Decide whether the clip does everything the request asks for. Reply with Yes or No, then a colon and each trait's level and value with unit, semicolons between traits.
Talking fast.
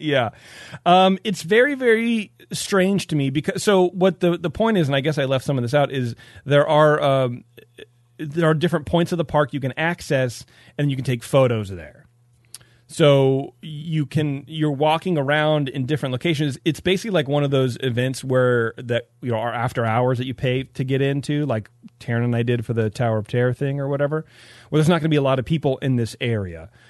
Yes: fast, 225 wpm